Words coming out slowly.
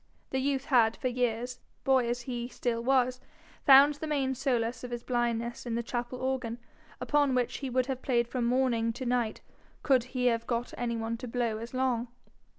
No: average, 195 wpm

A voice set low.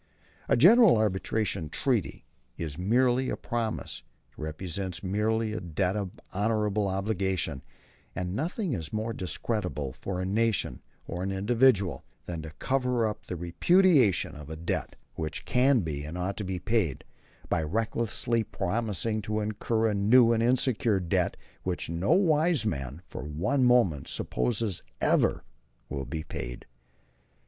Yes: low, 105 Hz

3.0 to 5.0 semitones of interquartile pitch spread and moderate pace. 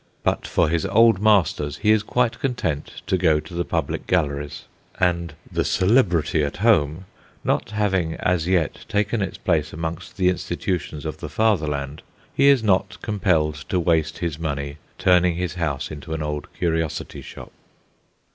Yes: average, 4.1 semitones; average, 160 wpm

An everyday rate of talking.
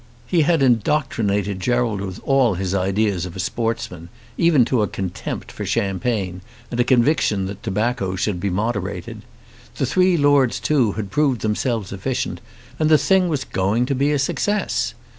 Yes: average, 165 wpm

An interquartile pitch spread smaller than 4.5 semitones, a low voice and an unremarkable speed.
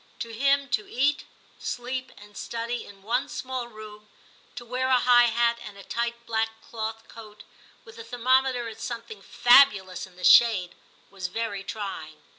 No: narrow, 2.6 semitones; high, 230 Hz; average, 165 wpm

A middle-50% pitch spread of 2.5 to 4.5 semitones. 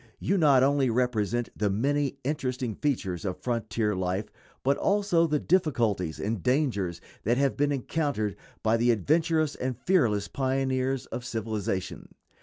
No: average, 5.1 semitones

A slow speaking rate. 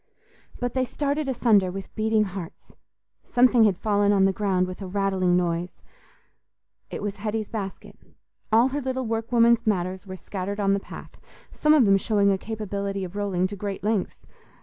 No: average, 170 wpm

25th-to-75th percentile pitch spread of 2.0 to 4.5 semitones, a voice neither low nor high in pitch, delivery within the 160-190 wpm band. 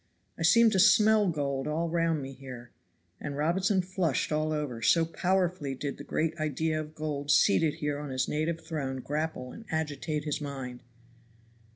Yes: average, 2.9 semitones; medium, 155 Hz; average, 170 wpm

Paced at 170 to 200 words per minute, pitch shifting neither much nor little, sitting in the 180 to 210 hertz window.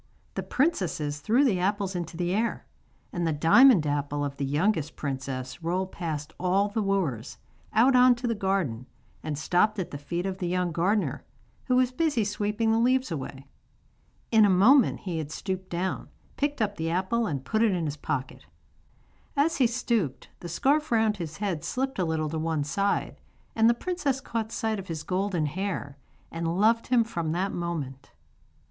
No: average, 185 wpm; wide, 5.9 semitones; medium, 185 Hz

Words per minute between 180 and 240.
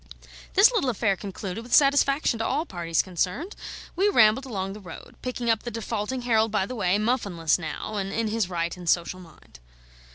Yes: average, 190 wpm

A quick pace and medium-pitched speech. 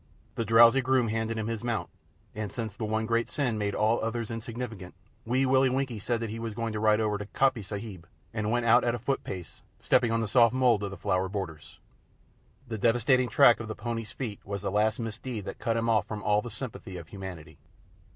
No: fast, 220 wpm; low, 115 Hz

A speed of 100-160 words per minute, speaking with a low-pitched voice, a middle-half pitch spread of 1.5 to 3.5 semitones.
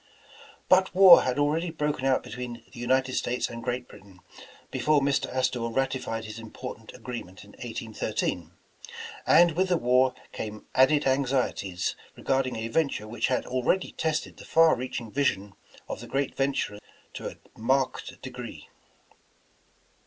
Yes: average, 145 wpm; low, 130 Hz; average, 3.2 semitones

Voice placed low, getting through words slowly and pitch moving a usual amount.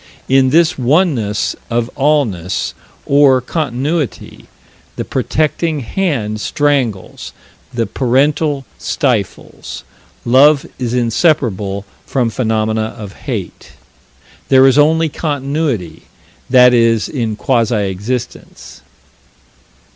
Yes: low, 130 Hz; slow, 90 wpm; average, 4.8 semitones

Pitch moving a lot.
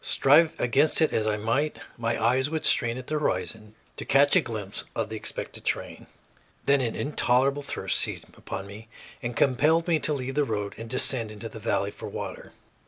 No: average, 4.6 semitones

